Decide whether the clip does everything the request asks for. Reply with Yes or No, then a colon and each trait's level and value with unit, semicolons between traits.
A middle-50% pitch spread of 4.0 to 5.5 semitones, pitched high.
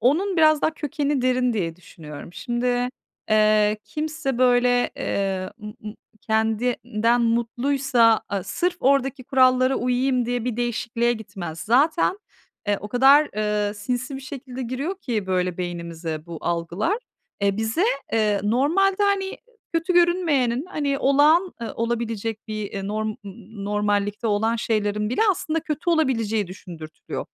Yes: average, 4.8 semitones; high, 235 Hz